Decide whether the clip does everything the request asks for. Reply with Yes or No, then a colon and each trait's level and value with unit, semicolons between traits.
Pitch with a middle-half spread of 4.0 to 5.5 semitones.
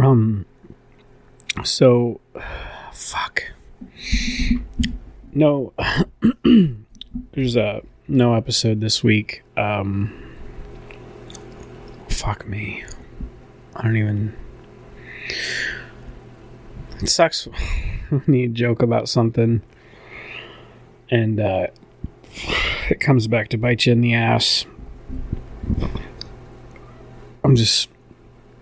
No: average, 3.3 semitones